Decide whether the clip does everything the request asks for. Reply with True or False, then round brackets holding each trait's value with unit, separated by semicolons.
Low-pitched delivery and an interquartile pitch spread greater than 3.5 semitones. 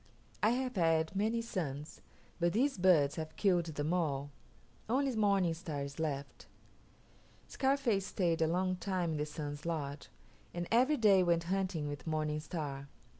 False (170 Hz; 4.5 semitones)